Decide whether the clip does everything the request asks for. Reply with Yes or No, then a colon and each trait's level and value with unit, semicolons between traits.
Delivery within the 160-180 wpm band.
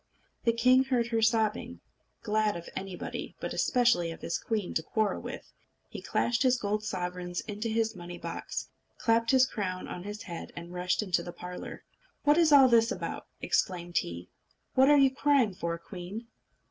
Yes: average, 175 wpm